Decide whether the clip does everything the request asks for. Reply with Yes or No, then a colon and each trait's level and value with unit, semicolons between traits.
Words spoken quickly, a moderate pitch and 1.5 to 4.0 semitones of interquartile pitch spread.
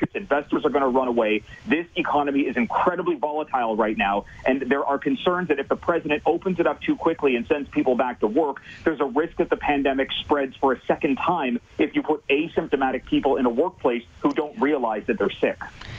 Yes: fast, 220 wpm; medium, 145 Hz; average, 3.3 semitones